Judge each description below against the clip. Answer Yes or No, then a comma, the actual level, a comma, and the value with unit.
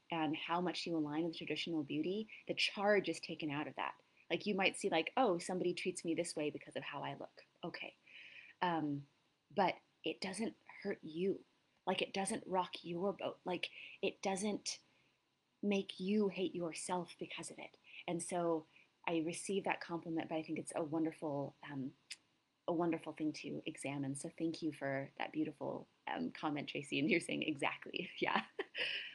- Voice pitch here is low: No, medium, 165 Hz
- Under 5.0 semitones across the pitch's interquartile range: Yes, average, 2.8 semitones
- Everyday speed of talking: Yes, average, 175 wpm